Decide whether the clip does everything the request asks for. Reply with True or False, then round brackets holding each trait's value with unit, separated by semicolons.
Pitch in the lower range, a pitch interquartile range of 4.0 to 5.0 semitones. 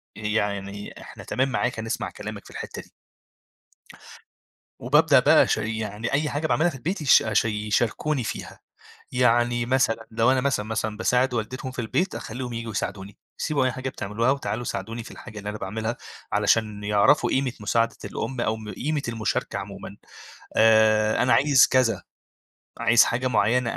False (115 Hz; 3.2 semitones)